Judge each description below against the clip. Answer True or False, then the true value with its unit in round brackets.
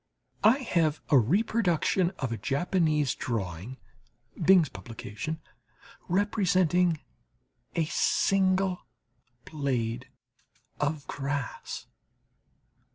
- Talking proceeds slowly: True (75 wpm)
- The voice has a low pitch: False (155 Hz)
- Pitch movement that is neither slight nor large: False (5.9 semitones)